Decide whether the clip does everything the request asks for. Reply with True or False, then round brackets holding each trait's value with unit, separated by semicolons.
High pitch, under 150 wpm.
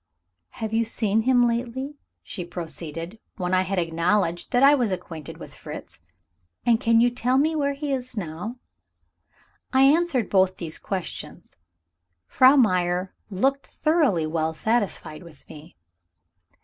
True (215 Hz; 140 wpm)